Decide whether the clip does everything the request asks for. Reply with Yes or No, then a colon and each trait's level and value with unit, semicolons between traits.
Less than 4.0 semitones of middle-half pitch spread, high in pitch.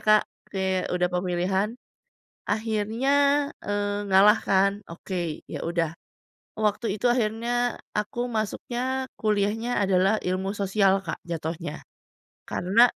Yes: average, 2.9 semitones; high, 205 Hz